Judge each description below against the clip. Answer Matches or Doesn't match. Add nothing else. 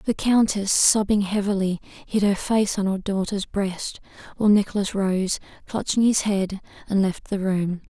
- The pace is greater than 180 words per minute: Doesn't match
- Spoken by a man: Doesn't match